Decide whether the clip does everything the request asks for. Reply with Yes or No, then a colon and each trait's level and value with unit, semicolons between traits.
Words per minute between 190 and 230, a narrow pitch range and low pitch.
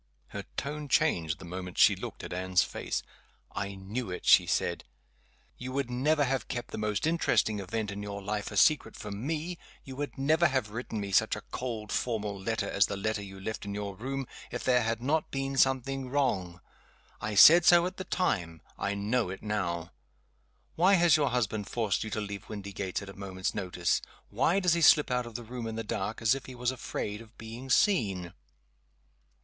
No: average, 200 wpm; average, 5.2 semitones; low, 110 Hz